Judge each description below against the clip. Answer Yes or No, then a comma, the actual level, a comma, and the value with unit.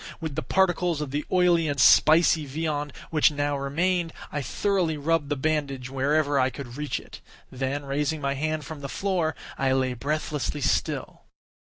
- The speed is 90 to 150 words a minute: No, average, 170 wpm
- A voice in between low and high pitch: Yes, medium, 150 Hz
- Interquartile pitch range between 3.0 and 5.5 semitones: No, narrow, 2.5 semitones